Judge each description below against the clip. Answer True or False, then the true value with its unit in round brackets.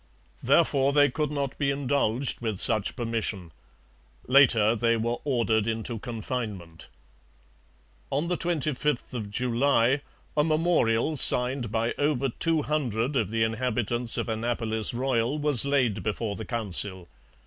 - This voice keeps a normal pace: False (130 wpm)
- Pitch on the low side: True (120 Hz)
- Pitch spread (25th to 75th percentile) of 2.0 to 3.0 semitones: False (3.9 semitones)